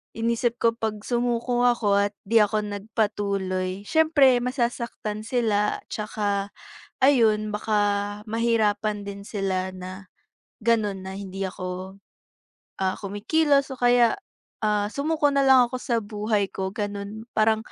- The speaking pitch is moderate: No, high, 215 Hz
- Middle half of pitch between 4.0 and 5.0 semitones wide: No, average, 2.8 semitones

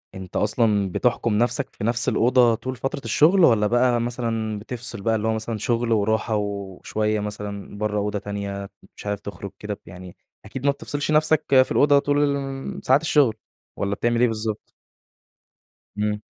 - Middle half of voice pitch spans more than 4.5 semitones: No, average, 3.1 semitones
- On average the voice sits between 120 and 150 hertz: No, low, 110 Hz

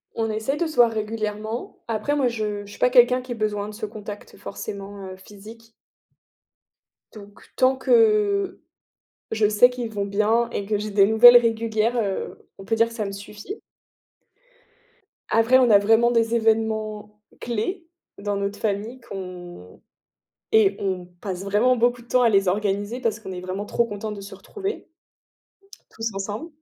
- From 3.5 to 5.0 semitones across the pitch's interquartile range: No, average, 2.7 semitones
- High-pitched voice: Yes, high, 220 Hz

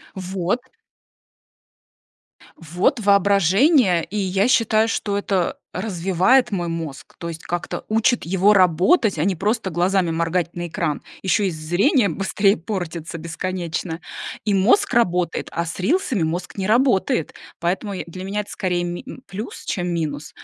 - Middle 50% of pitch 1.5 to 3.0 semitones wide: No, average, 3.4 semitones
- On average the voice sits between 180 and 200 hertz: Yes, medium, 185 Hz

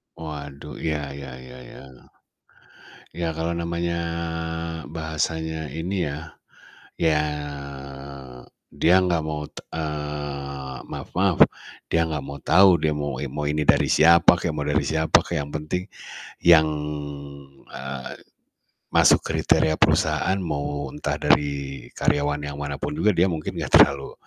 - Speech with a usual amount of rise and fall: No, narrow, 2.3 semitones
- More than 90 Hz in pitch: No, very low, 75 Hz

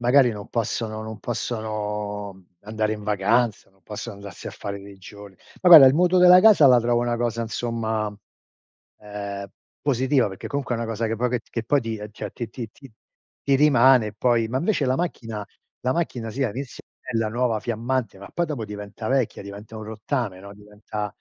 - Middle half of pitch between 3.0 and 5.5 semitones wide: Yes, average, 3.4 semitones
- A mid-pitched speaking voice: No, low, 115 Hz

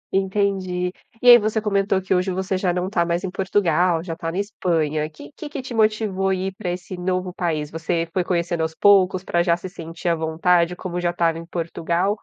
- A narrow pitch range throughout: Yes, narrow, 2.3 semitones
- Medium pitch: Yes, medium, 180 Hz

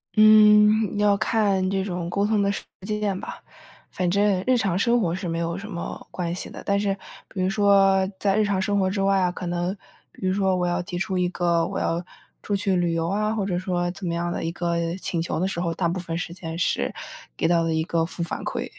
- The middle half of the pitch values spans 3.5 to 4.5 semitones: No, narrow, 2.6 semitones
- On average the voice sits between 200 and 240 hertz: No, medium, 185 Hz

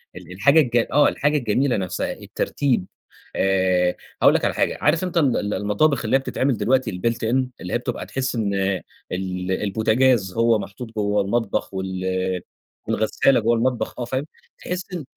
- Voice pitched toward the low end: Yes, low, 115 Hz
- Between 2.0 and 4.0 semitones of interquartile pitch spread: No, wide, 5.4 semitones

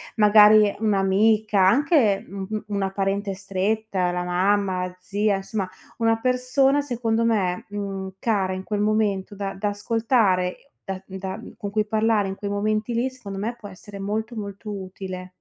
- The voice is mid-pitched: No, high, 205 Hz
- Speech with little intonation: Yes, narrow, 2.3 semitones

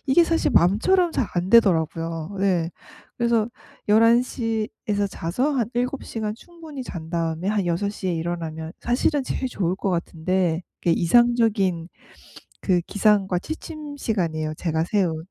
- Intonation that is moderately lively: No, wide, 5.9 semitones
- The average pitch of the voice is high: Yes, high, 200 Hz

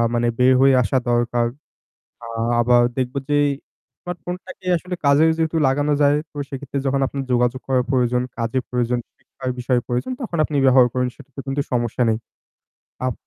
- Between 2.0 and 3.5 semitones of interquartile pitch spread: Yes, narrow, 2.5 semitones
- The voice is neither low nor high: No, low, 130 Hz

